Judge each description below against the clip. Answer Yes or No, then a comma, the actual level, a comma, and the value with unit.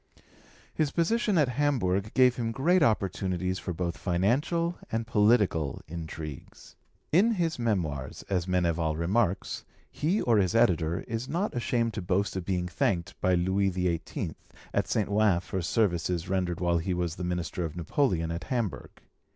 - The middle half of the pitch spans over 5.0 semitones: Yes, wide, 5.5 semitones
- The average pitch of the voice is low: Yes, very low, 95 Hz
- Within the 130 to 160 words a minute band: Yes, average, 155 wpm